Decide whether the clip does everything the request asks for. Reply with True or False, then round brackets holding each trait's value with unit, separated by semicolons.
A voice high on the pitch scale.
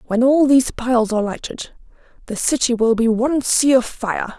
True (245 Hz)